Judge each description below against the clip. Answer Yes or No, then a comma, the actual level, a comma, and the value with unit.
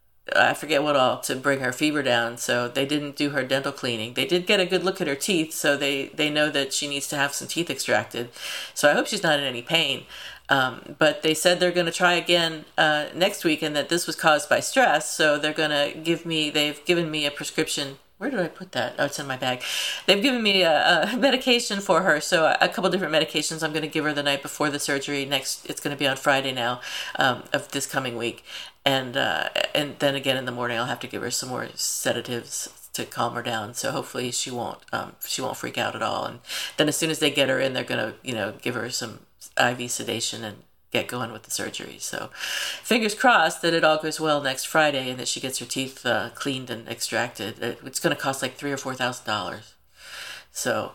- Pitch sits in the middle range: Yes, medium, 145 Hz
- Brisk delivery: Yes, fast, 245 wpm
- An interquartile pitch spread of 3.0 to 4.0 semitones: Yes, average, 3.6 semitones